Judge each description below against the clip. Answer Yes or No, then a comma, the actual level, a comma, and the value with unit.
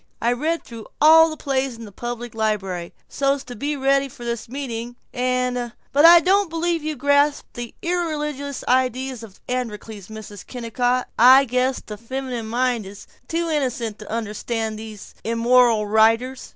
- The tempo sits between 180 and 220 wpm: No, average, 165 wpm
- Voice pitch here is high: Yes, very high, 250 Hz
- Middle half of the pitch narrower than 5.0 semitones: Yes, average, 3.6 semitones